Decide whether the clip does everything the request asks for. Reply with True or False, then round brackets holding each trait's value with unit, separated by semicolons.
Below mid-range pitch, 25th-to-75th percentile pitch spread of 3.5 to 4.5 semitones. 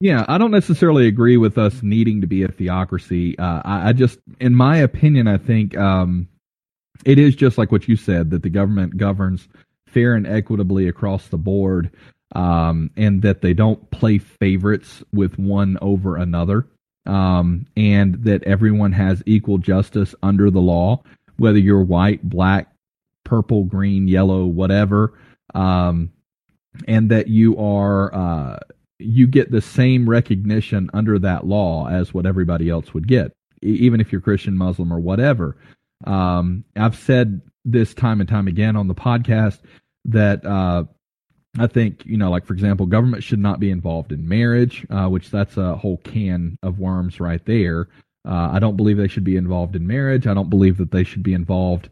False (100 Hz; 3.1 semitones)